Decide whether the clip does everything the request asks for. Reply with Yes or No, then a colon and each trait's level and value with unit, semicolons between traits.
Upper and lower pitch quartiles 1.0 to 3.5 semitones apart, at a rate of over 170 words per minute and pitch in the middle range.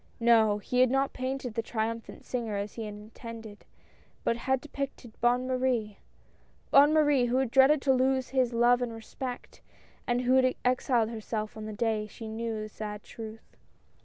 No: average, 2.8 semitones; average, 180 wpm; high, 235 Hz